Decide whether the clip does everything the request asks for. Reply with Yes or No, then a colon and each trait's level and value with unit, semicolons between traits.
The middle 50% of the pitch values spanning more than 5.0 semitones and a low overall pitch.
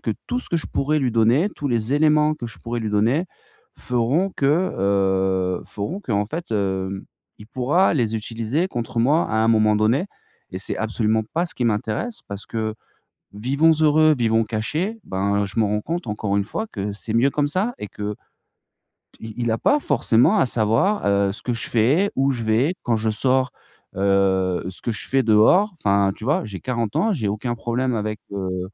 Yes: wide, 5.6 semitones; low, 115 Hz